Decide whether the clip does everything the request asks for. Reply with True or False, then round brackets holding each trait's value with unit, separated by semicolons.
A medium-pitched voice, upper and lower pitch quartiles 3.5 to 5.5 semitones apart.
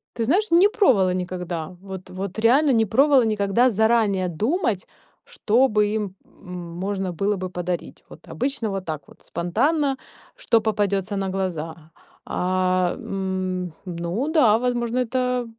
False (200 Hz; 4.9 semitones)